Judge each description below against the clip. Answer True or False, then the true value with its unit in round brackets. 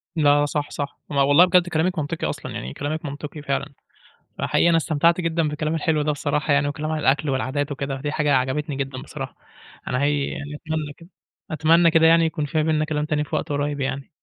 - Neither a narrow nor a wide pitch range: False (1.8 semitones)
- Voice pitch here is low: False (150 Hz)